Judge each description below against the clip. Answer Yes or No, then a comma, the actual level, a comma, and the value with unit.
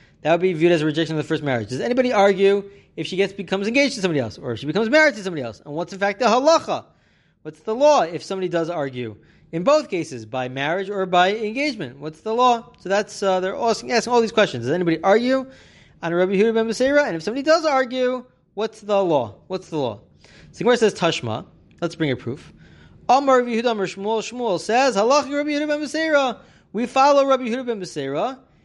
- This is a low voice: No, high, 200 Hz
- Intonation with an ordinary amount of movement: No, wide, 6.8 semitones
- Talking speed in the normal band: No, fast, 210 wpm